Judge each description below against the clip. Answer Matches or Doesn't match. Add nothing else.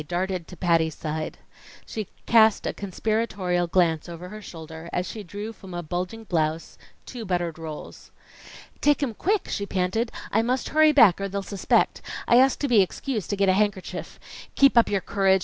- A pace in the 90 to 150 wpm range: Doesn't match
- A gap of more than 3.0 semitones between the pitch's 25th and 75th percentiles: Matches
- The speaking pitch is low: Doesn't match